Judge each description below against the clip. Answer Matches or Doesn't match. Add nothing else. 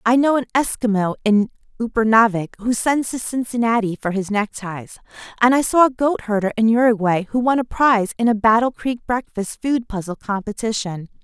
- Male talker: Doesn't match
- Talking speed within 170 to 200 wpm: Matches